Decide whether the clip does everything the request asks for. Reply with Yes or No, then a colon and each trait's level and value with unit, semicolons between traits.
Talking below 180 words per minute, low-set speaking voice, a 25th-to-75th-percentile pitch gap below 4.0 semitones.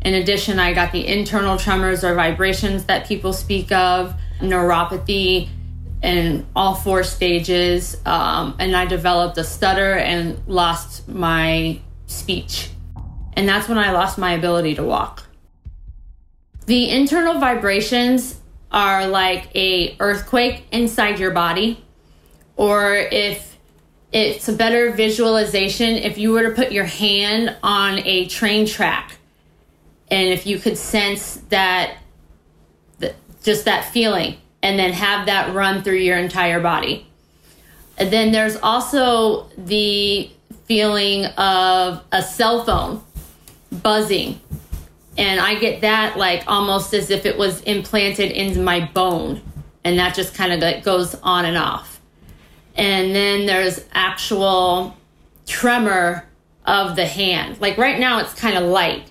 No: slow, 135 wpm; high, 190 Hz; average, 2.9 semitones